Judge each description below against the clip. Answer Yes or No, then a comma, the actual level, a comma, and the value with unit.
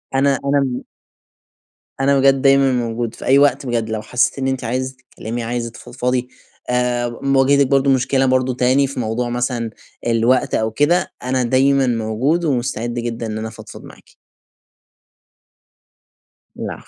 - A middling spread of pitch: No, narrow, 2.3 semitones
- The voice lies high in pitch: No, low, 125 Hz